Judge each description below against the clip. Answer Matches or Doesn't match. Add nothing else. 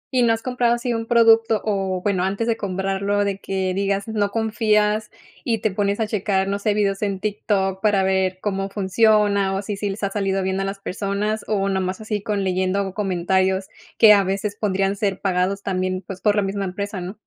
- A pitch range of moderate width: Doesn't match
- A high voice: Matches